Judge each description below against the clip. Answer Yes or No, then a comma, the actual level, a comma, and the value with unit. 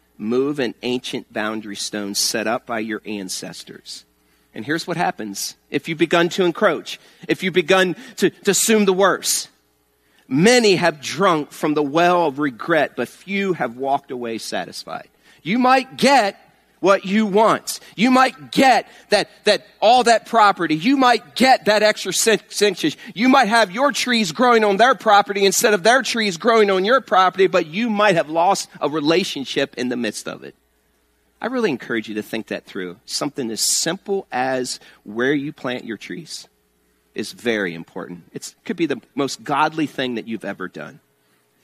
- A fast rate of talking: No, average, 185 wpm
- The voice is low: No, medium, 170 Hz